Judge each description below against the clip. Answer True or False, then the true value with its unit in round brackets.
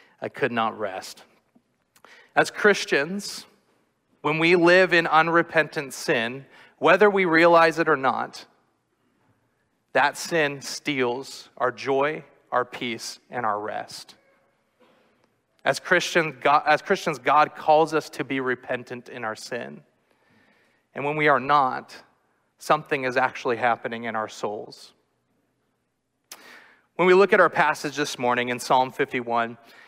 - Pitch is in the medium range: True (150 Hz)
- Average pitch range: True (4.7 semitones)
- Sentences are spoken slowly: True (125 wpm)